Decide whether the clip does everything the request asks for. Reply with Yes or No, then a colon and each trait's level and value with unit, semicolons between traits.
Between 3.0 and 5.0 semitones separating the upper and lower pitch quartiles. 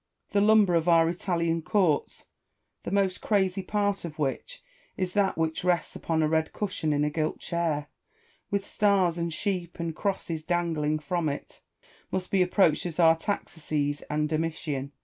Yes: average, 3.4 semitones